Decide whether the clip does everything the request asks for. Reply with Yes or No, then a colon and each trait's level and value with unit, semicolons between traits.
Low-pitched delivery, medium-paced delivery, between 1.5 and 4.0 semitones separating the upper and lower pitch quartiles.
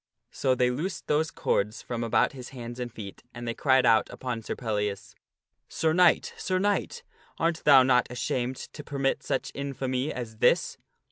Yes: low, 125 Hz; average, 180 wpm; average, 3.6 semitones